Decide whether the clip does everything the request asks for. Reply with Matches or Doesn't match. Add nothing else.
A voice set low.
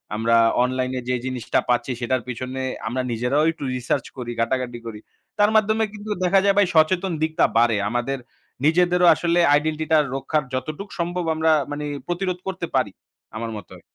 Doesn't match